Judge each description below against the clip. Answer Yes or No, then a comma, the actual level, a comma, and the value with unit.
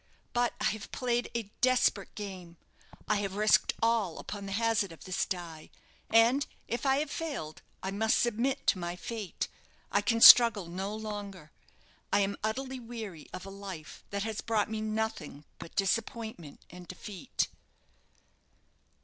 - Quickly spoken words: No, average, 155 wpm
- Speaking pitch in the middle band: No, high, 210 Hz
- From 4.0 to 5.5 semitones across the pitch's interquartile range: No, average, 3.4 semitones